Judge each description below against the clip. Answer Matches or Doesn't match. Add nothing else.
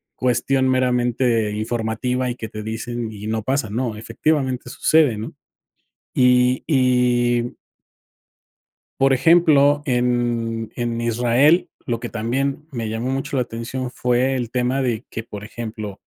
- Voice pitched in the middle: Doesn't match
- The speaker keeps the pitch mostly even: Matches